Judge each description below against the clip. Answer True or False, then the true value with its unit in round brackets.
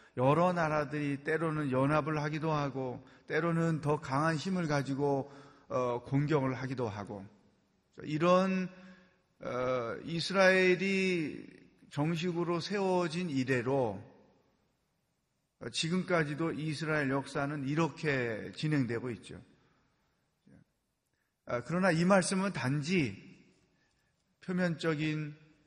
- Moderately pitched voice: True (155 Hz)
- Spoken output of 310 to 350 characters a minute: False (205 characters per minute)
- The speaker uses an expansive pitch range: False (4.1 semitones)